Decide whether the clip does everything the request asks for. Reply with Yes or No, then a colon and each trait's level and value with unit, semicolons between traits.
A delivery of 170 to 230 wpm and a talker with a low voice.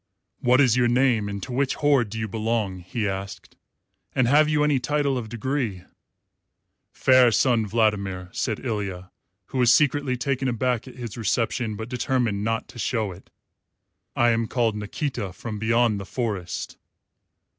No: average, 160 wpm; low, 115 Hz